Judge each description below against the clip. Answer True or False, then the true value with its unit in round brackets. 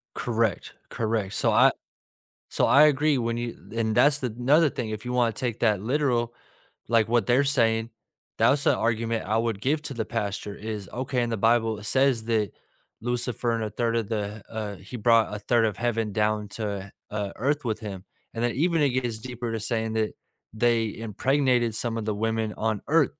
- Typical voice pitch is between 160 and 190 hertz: False (115 Hz)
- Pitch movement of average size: False (2.1 semitones)